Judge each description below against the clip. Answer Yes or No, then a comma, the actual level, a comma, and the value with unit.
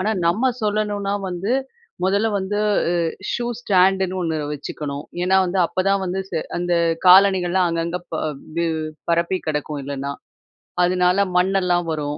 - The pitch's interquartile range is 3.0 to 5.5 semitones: No, narrow, 2.4 semitones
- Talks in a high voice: No, medium, 180 Hz